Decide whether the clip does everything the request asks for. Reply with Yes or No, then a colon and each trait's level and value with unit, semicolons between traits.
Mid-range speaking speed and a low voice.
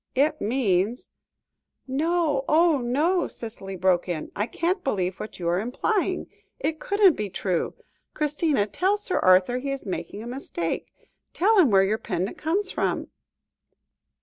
No: average, 150 wpm; very high, 250 Hz